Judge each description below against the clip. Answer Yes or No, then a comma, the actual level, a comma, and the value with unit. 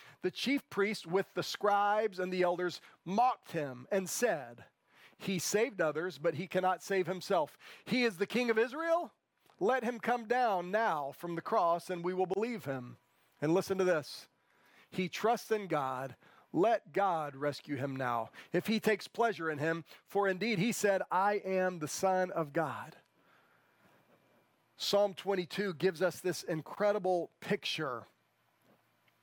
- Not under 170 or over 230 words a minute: No, average, 155 wpm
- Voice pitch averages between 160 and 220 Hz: Yes, medium, 185 Hz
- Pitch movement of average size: Yes, average, 4.1 semitones